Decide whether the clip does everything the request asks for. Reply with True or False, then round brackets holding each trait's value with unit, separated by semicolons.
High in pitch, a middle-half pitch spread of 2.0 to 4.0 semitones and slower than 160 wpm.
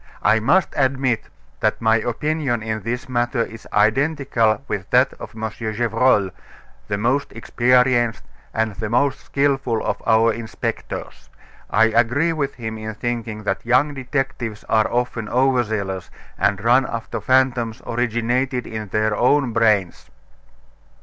False (115 Hz; 2.8 semitones; 135 wpm)